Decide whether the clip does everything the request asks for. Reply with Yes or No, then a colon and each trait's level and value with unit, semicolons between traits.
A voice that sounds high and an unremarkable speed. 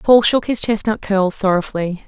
Yes: high, 205 Hz; average, 175 wpm